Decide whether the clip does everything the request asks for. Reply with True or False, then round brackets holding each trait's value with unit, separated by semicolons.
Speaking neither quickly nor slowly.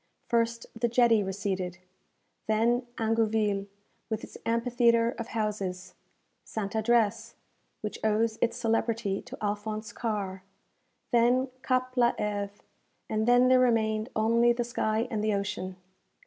False (125 wpm)